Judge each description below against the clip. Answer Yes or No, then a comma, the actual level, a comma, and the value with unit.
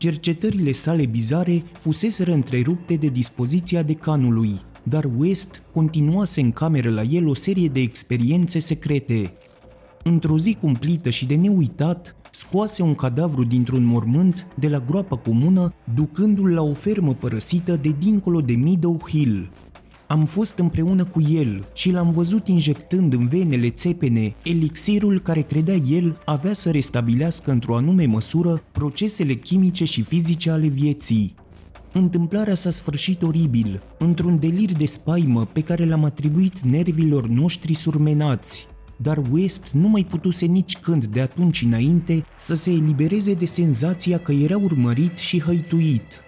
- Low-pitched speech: No, medium, 160 Hz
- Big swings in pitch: No, average, 4.6 semitones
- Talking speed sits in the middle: Yes, average, 140 wpm